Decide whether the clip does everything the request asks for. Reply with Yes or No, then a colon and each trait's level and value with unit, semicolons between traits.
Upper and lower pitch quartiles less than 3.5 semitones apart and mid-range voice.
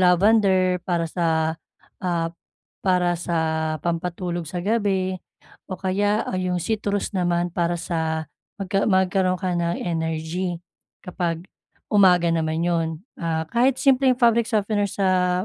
Yes: average, 2.7 semitones; medium, 180 Hz